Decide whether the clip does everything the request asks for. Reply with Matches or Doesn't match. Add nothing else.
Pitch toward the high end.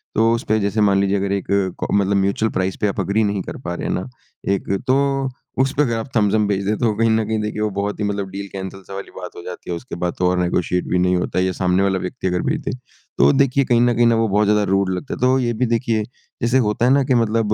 Doesn't match